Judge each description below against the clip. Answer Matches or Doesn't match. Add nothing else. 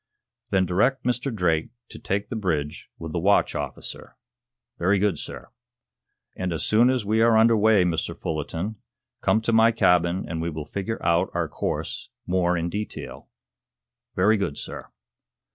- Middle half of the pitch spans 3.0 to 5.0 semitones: Matches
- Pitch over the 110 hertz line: Doesn't match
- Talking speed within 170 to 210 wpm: Doesn't match